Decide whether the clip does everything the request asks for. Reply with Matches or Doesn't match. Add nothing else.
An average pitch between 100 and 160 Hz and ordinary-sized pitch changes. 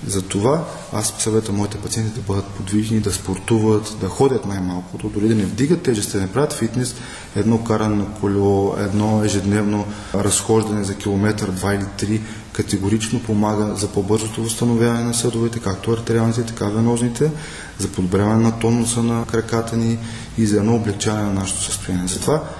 Doesn't match